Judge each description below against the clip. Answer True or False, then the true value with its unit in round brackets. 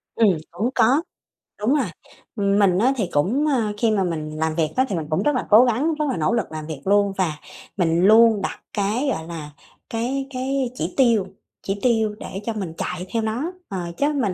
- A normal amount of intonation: False (5.8 semitones)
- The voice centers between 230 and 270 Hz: False (210 Hz)